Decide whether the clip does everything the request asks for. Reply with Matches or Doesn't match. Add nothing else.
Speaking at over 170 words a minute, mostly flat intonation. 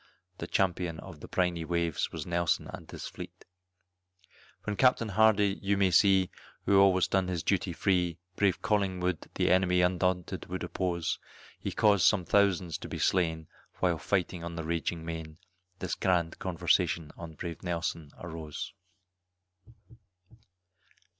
Doesn't match